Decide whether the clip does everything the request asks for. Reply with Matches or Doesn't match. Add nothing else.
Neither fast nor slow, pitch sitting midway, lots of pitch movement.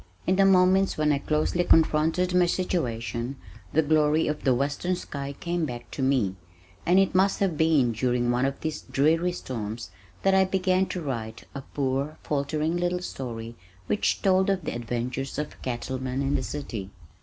Matches